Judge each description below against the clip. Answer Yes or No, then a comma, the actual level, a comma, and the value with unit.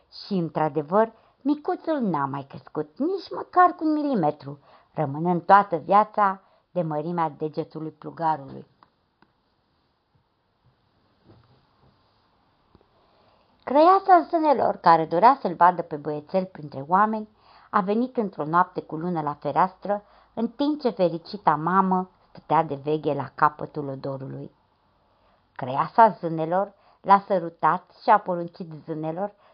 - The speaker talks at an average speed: No, slow, 110 wpm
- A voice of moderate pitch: Yes, medium, 180 Hz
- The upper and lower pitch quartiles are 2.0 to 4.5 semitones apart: No, average, 5.3 semitones